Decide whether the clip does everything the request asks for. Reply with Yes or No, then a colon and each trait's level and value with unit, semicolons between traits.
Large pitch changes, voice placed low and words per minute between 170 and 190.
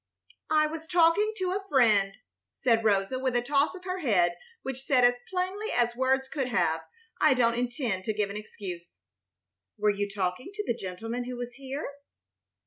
No: wide, 6.3 semitones; high, 245 Hz; average, 185 wpm